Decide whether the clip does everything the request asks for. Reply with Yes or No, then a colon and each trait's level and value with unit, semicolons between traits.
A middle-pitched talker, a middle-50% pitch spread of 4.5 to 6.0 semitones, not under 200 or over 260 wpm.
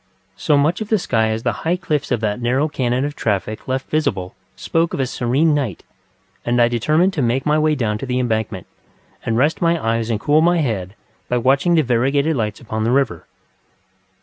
No: low, 130 Hz; average, 5.1 semitones; fast, 205 wpm